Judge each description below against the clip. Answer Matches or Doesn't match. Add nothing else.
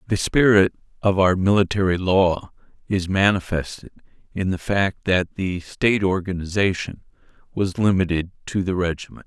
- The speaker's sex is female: Doesn't match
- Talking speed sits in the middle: Doesn't match